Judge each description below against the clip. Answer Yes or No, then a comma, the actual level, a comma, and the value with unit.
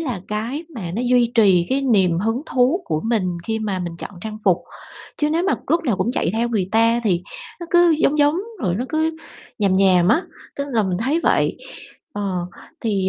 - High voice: Yes, high, 225 Hz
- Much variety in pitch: Yes, wide, 6.0 semitones